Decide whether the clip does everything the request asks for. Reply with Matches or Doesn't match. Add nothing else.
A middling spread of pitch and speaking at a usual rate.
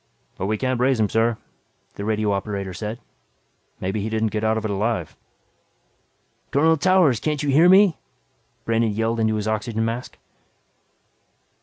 Matches